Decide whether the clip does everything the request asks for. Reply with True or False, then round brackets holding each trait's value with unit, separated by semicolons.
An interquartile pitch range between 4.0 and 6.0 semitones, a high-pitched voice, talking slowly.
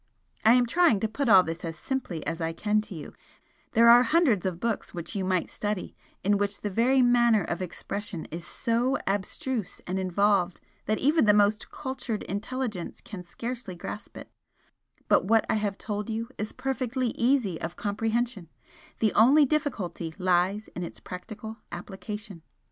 False (4.3 semitones; 210 Hz; 170 wpm)